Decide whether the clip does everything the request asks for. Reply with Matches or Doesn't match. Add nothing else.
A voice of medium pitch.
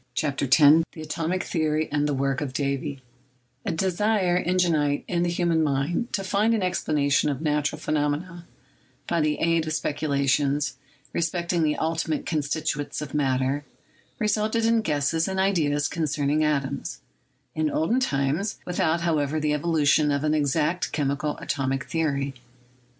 Matches